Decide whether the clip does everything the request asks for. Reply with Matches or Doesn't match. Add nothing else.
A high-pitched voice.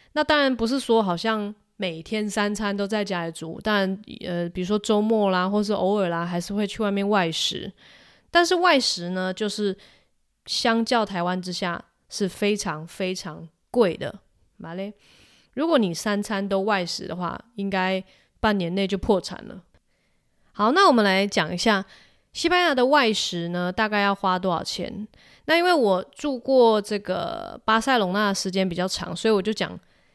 Matches